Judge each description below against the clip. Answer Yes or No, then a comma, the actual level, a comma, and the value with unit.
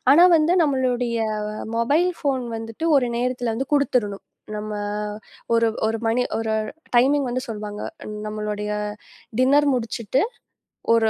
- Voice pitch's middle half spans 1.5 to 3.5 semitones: Yes, average, 3.1 semitones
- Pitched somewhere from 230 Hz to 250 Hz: Yes, high, 240 Hz